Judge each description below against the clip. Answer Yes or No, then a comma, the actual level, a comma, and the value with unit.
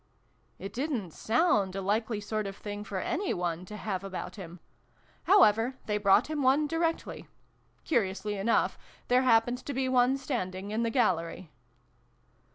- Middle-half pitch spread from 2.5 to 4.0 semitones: No, average, 4.8 semitones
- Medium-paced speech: Yes, average, 165 wpm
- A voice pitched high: Yes, high, 215 Hz